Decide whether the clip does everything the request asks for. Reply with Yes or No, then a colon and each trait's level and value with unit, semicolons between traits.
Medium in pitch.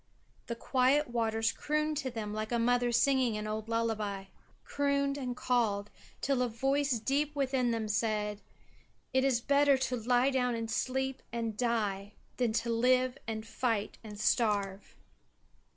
No: high, 235 Hz